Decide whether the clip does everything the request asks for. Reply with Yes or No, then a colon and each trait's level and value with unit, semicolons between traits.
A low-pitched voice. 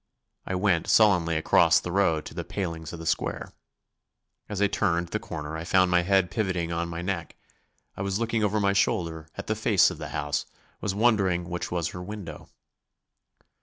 Yes: very low, 90 Hz